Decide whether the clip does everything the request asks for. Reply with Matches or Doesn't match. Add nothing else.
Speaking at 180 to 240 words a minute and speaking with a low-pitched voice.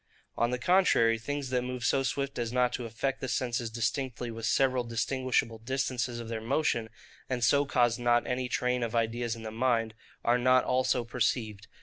Matches